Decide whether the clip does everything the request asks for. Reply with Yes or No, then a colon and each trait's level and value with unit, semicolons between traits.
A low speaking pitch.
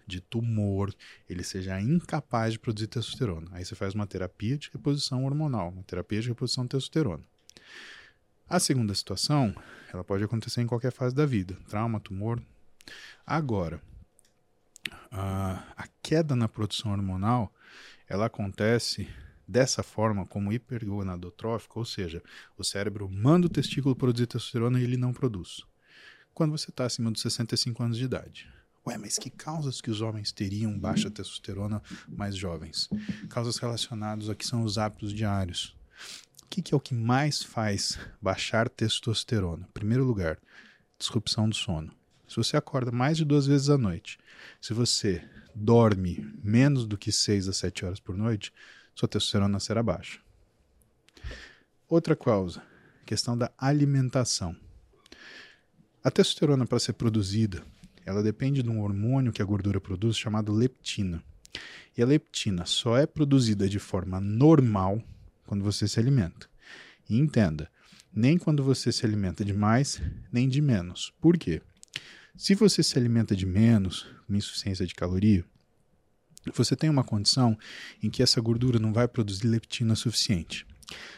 Yes: low, 110 Hz